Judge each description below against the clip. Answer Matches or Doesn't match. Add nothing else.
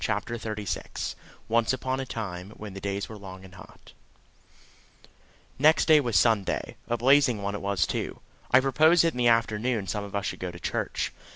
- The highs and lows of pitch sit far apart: Doesn't match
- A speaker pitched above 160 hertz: Doesn't match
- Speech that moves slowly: Doesn't match